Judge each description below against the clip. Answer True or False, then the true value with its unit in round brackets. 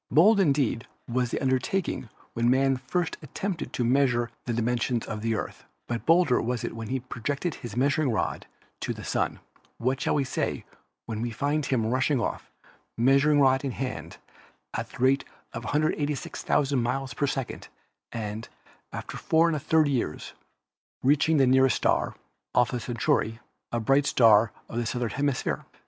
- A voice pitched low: True (130 Hz)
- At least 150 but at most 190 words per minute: True (160 wpm)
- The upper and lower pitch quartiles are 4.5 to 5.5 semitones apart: False (3.3 semitones)